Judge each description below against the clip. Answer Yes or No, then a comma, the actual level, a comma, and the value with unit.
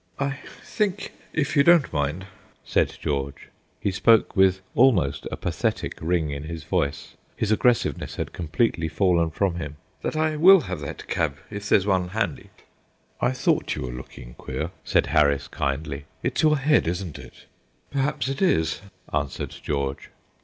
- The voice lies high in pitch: No, very low, 90 Hz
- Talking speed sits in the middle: Yes, average, 160 wpm